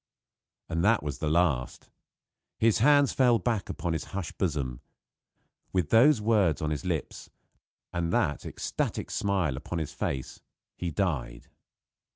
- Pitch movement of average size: No, wide, 5.7 semitones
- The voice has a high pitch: No, very low, 85 Hz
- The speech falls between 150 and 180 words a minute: No, average, 140 wpm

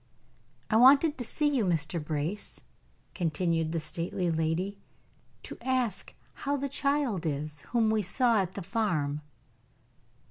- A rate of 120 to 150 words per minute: Yes, slow, 135 wpm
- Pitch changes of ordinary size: No, wide, 7.2 semitones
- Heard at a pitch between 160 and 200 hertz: Yes, high, 190 Hz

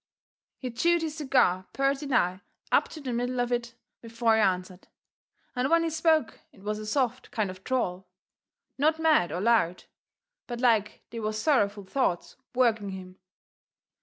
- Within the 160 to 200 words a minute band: Yes, average, 170 wpm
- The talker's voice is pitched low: No, high, 235 Hz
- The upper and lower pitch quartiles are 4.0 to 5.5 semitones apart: Yes, average, 5.2 semitones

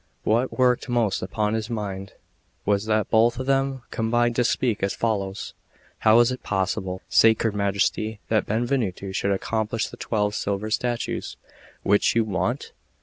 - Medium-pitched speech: No, low, 110 Hz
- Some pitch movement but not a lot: Yes, average, 3.0 semitones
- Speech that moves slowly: No, average, 150 wpm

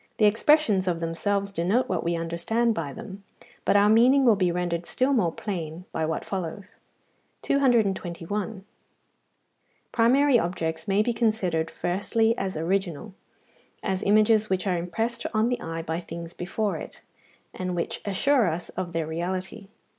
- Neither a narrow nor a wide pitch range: Yes, average, 4.6 semitones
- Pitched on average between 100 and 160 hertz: No, high, 190 Hz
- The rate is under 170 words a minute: Yes, average, 150 wpm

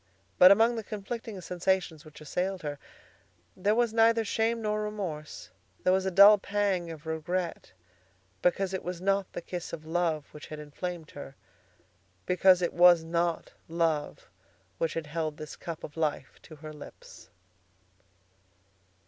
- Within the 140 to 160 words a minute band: Yes, average, 150 wpm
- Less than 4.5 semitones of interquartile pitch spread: Yes, average, 3.8 semitones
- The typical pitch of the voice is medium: Yes, medium, 175 Hz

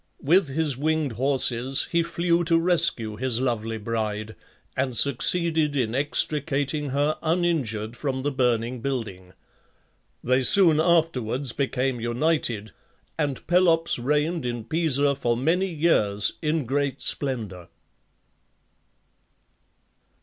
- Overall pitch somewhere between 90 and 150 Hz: Yes, low, 135 Hz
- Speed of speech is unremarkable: No, slow, 110 wpm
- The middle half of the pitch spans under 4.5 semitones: No, average, 5.1 semitones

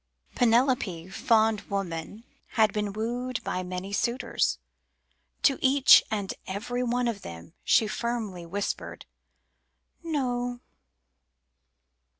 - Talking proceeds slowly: Yes, slow, 100 wpm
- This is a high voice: Yes, high, 220 Hz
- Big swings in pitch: No, average, 3.9 semitones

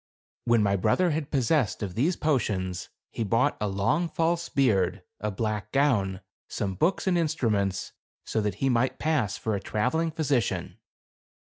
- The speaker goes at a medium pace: Yes, average, 155 wpm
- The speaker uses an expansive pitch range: Yes, wide, 7.2 semitones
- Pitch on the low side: Yes, low, 115 Hz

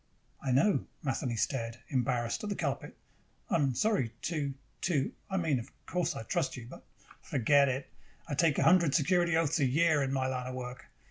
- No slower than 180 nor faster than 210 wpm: Yes, average, 195 wpm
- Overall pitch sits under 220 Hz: Yes, medium, 140 Hz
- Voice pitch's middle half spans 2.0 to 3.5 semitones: No, average, 4.5 semitones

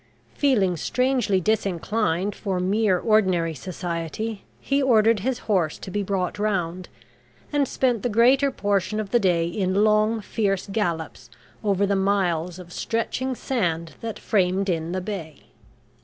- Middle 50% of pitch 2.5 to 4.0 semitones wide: Yes, average, 3.5 semitones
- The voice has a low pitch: No, high, 200 Hz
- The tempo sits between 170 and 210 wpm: No, average, 140 wpm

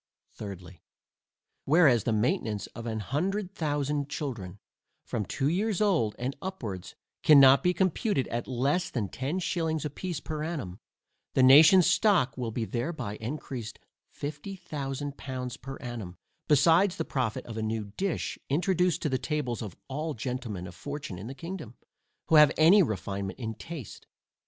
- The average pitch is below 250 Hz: Yes, low, 135 Hz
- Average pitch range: No, wide, 6.4 semitones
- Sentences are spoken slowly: No, average, 155 wpm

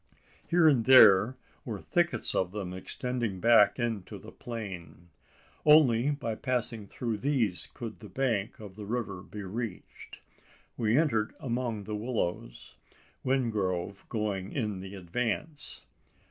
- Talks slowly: Yes, slow, 130 wpm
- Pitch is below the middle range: Yes, low, 110 Hz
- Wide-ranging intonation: No, average, 4.1 semitones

